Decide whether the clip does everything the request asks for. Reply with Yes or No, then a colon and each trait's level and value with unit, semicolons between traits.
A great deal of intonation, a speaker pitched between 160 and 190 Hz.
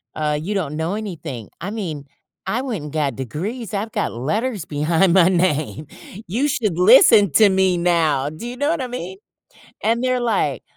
Yes: wide, 6.3 semitones; medium, 185 Hz